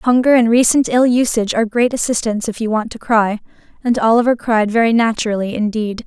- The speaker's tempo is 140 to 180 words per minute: No, average, 190 wpm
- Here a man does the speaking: No, female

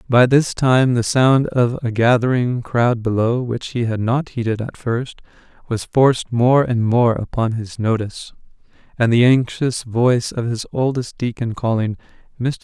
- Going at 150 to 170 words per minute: Yes, average, 165 wpm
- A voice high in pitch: No, low, 120 Hz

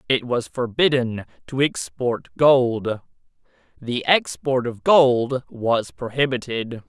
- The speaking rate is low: Yes, slow, 105 wpm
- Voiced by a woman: No, male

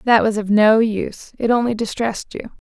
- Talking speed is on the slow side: No, average, 200 wpm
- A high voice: Yes, high, 220 Hz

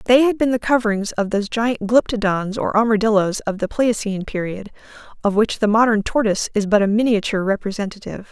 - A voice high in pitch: Yes, high, 215 Hz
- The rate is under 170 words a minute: No, average, 180 wpm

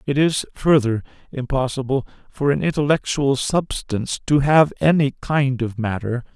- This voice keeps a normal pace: No, slow, 130 wpm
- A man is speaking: Yes, male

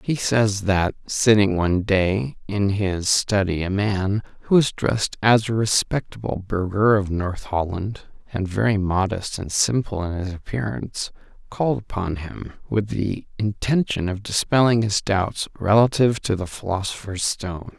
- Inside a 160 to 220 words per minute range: No, average, 150 wpm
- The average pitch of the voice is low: Yes, low, 100 Hz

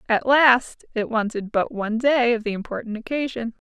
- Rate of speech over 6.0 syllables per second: No, 5.1 syllables/s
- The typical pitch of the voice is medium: No, high, 235 Hz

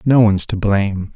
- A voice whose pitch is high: No, low, 100 Hz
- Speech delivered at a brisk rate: Yes, fast, 210 wpm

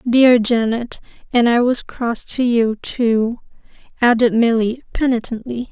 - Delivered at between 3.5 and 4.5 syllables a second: Yes, 4.0 syllables/s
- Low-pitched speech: No, high, 235 Hz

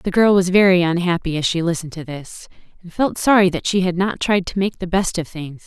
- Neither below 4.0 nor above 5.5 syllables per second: No, 5.7 syllables/s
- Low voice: No, medium, 180 Hz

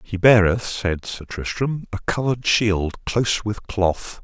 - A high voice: No, low, 105 Hz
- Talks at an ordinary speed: Yes, average, 155 wpm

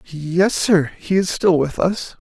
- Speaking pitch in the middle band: Yes, medium, 175 Hz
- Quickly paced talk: No, average, 185 wpm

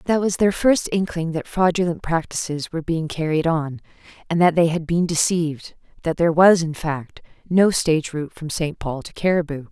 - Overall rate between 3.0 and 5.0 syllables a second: No, 5.3 syllables/s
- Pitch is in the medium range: Yes, medium, 165 Hz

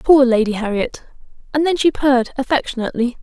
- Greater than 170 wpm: No, average, 150 wpm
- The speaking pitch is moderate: No, very high, 260 Hz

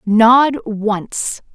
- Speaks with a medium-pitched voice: No, high, 225 Hz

